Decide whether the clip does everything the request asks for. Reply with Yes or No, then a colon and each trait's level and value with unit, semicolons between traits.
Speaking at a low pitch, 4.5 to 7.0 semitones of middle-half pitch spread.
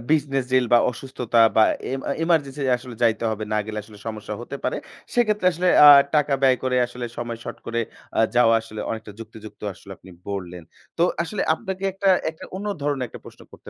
Yes: low, 125 Hz; average, 5.1 semitones